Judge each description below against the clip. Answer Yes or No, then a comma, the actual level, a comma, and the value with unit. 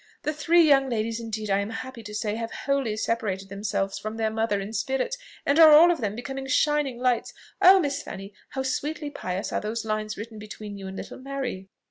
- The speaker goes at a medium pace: No, fast, 210 wpm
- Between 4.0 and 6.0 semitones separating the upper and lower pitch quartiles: Yes, average, 4.7 semitones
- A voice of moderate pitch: No, high, 230 Hz